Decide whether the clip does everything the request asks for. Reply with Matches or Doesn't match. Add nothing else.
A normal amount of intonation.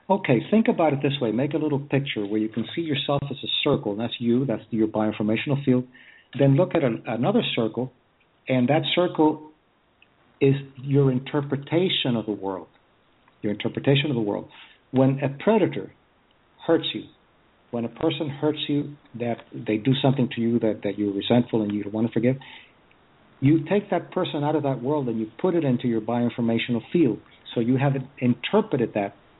Matches